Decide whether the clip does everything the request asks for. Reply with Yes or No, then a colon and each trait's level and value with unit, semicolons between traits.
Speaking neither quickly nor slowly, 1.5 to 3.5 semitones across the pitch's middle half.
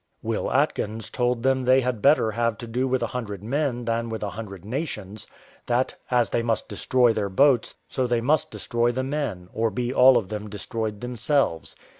Yes: average, 195 wpm; average, 2.9 semitones